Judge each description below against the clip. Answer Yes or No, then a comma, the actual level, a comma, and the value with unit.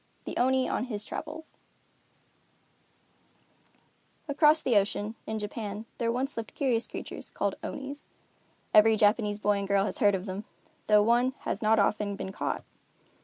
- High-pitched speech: Yes, high, 220 Hz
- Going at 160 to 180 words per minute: No, average, 150 wpm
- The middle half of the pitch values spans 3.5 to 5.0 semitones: Yes, average, 3.8 semitones